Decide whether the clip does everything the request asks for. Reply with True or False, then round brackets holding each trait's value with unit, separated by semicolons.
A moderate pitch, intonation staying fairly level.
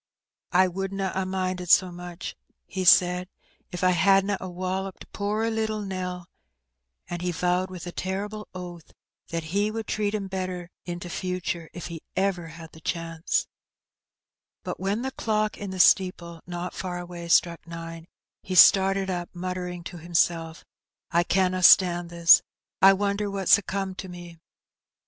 True (180 Hz; 1.8 semitones)